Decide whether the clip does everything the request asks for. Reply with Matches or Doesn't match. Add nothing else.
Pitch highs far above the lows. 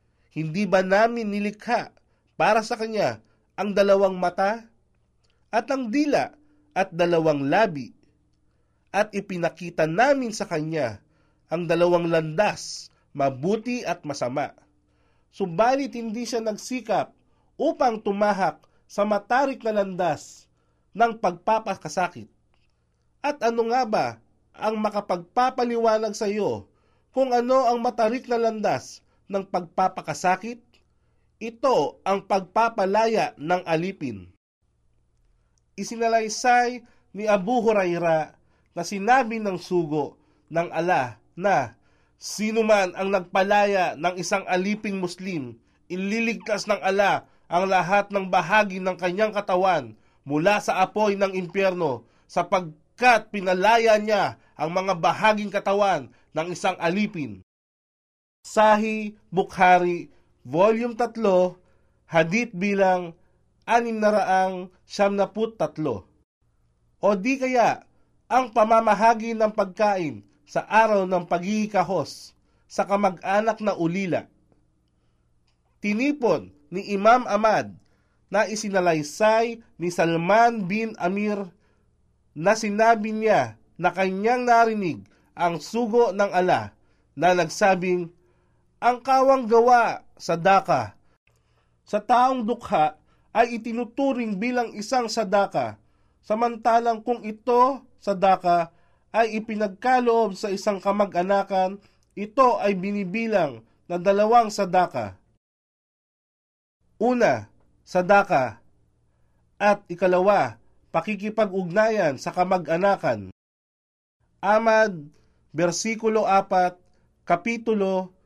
Doesn't match